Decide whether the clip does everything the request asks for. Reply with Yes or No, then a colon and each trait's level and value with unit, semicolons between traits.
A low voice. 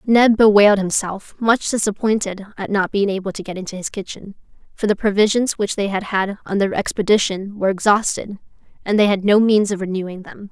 No: high, 200 Hz